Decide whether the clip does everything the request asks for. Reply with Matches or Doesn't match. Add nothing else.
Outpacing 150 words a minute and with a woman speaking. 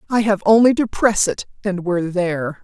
Matches